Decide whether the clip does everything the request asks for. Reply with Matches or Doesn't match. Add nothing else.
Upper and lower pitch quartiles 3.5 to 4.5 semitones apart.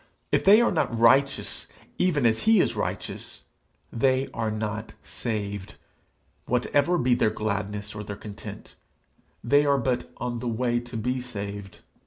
Matches